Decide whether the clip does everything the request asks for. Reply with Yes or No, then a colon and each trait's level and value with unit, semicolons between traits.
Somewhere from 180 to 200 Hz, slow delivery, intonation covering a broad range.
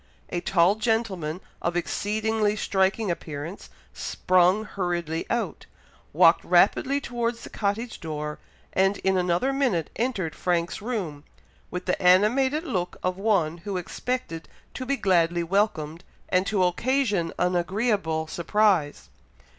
No: high, 190 Hz; slow, 125 wpm; average, 4.2 semitones